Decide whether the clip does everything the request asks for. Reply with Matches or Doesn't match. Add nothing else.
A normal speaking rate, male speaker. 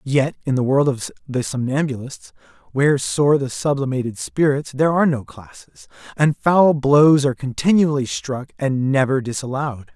Matches